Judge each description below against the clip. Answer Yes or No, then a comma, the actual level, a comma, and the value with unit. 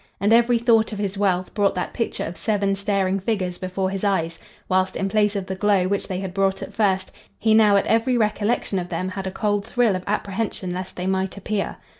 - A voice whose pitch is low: No, high, 195 Hz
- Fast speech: Yes, fast, 225 wpm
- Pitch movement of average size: No, narrow, 2.1 semitones